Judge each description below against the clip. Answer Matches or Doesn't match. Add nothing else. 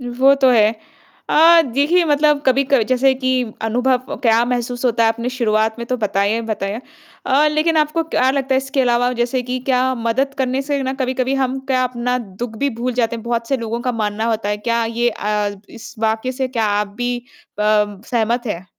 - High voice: Matches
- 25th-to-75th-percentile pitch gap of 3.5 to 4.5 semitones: Doesn't match